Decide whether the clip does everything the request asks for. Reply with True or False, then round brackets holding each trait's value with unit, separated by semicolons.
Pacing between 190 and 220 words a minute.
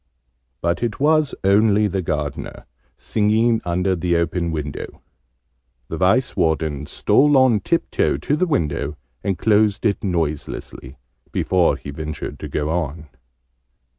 False (135 wpm)